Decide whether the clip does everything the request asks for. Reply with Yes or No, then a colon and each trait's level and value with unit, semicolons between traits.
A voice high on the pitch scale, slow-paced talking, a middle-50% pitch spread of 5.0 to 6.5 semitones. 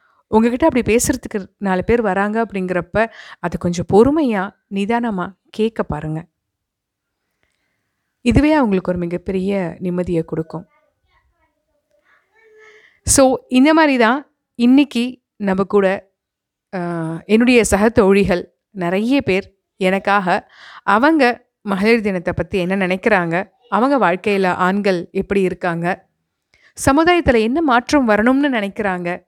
No: high, 205 Hz; average, 95 wpm; wide, 5.4 semitones